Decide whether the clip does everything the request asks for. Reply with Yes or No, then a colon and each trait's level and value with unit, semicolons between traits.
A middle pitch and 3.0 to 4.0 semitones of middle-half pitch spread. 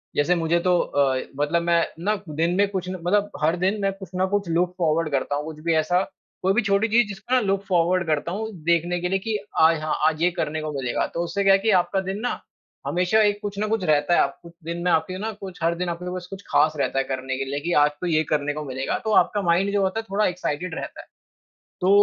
Yes: medium, 175 Hz; average, 3.7 semitones